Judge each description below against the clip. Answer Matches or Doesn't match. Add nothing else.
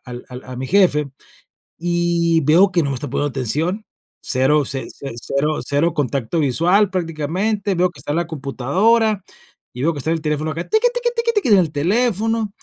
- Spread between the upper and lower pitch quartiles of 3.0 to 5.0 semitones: Doesn't match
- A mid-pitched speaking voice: Matches